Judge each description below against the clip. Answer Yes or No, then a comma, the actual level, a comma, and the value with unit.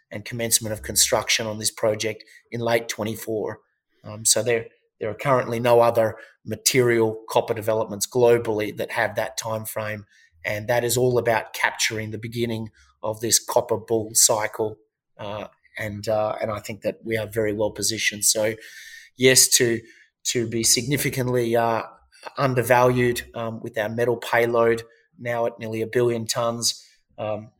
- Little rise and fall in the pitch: Yes, narrow, 1.7 semitones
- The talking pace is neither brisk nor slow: Yes, average, 155 wpm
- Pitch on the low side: Yes, low, 115 Hz